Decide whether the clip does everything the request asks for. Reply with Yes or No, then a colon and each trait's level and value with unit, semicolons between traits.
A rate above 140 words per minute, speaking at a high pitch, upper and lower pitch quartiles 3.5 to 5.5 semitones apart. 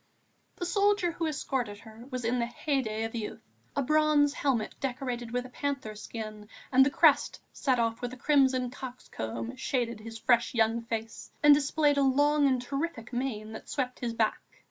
Yes: average, 185 wpm; very high, 250 Hz; average, 3.8 semitones